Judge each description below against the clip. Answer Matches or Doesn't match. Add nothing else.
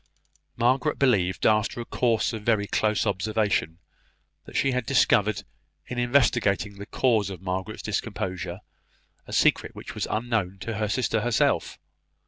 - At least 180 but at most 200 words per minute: Doesn't match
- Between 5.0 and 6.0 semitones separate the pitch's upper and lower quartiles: Doesn't match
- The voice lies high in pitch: Doesn't match